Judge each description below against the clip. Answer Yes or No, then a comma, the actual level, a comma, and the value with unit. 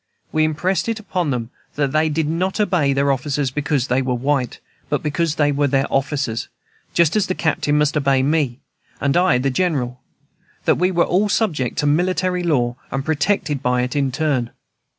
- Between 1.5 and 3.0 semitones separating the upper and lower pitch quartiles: No, average, 4.0 semitones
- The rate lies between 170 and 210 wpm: Yes, average, 190 wpm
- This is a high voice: No, medium, 145 Hz